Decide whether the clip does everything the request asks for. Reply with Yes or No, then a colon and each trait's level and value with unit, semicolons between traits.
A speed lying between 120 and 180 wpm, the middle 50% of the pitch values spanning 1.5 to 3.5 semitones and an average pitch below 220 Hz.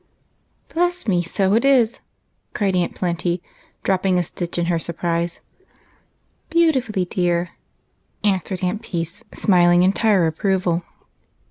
Yes: slow, 135 wpm; average, 3.2 semitones; medium, 185 Hz